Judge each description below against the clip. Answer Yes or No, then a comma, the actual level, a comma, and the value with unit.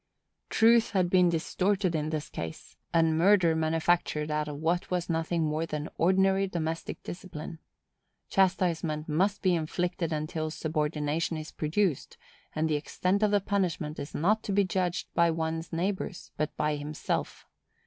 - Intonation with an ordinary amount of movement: Yes, average, 3.1 semitones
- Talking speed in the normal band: Yes, average, 155 wpm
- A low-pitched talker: No, medium, 165 Hz